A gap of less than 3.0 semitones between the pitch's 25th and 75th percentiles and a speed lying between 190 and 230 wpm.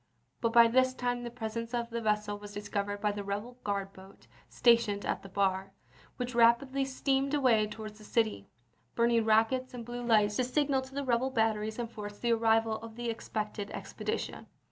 Yes: narrow, 2.6 semitones; average, 195 wpm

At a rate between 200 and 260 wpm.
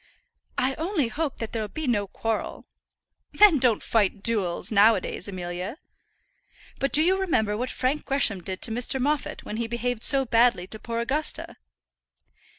No: average, 165 wpm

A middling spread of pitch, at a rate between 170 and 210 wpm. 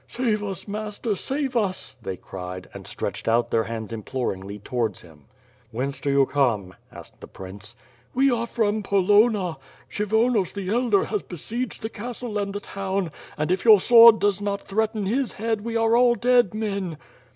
No: wide, 8.6 semitones; average, 175 wpm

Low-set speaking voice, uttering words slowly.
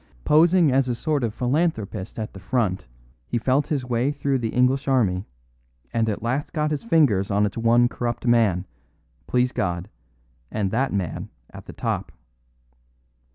No: low, 120 Hz; average, 160 wpm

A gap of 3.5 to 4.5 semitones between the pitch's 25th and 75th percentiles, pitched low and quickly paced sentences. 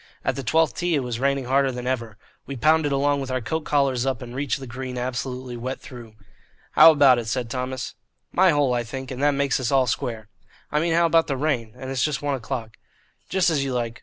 No: narrow, 2.6 semitones; low, 130 Hz; fast, 235 wpm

